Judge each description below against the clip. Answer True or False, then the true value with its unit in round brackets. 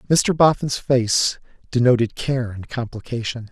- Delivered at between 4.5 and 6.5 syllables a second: False (4.3 syllables/s)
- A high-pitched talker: False (125 Hz)